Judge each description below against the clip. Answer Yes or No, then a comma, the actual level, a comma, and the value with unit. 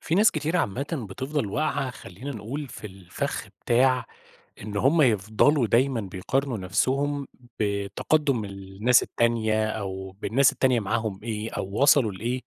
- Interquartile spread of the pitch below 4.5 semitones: No, average, 5.3 semitones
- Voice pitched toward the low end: Yes, low, 115 Hz